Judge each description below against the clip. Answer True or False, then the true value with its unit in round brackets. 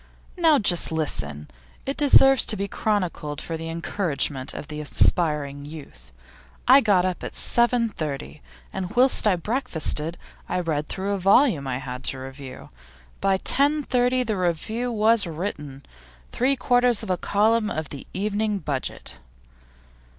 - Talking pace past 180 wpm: False (140 wpm)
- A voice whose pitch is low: False (185 Hz)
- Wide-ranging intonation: True (7.3 semitones)